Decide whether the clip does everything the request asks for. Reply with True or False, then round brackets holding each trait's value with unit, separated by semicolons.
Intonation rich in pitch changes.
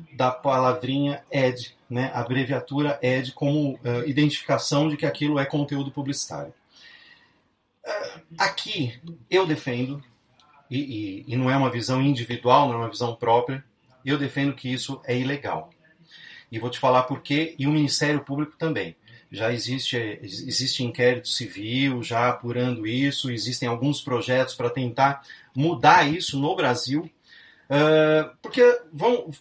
False (3.0 semitones)